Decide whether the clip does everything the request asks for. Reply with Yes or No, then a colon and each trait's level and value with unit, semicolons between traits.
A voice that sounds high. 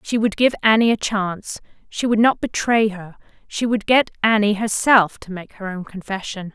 Yes: high, 210 Hz